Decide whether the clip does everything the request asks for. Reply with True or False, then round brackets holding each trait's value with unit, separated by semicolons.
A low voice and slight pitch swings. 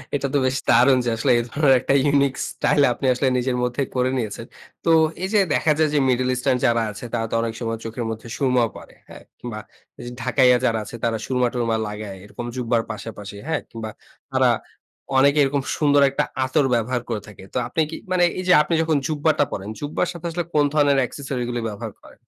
False (125 Hz; 3.7 semitones)